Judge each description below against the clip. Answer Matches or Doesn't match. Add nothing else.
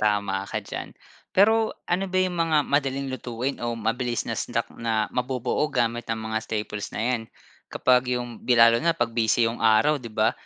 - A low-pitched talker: Matches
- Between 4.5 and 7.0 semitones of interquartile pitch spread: Doesn't match